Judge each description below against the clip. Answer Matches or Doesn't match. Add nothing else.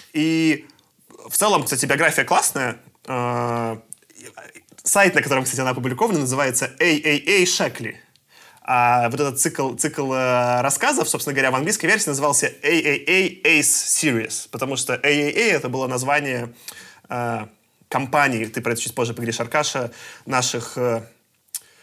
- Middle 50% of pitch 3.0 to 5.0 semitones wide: Matches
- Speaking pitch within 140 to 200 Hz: Doesn't match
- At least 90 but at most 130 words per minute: Matches